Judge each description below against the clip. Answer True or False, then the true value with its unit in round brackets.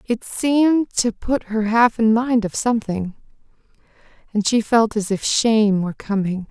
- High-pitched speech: True (220 Hz)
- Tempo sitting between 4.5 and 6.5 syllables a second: True (4.6 syllables/s)